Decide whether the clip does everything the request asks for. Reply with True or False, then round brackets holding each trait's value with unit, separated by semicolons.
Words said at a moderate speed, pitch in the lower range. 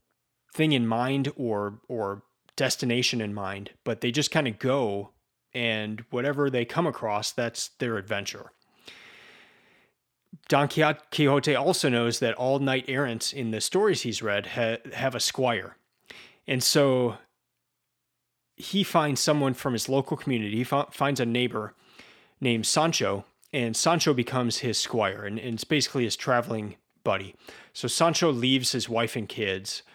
True (150 wpm; 125 Hz)